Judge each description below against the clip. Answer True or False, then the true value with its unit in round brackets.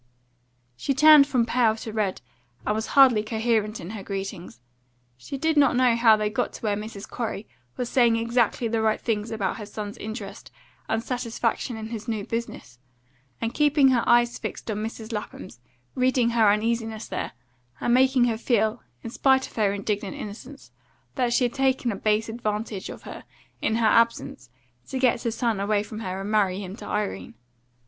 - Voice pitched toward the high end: True (225 Hz)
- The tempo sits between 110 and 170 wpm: False (185 wpm)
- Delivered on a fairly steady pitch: True (2.3 semitones)